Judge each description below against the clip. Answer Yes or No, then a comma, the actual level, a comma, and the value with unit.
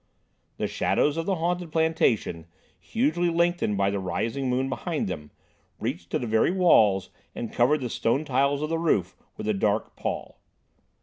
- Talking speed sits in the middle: Yes, average, 170 wpm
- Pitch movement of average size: No, wide, 7.8 semitones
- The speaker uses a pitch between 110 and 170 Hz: Yes, low, 135 Hz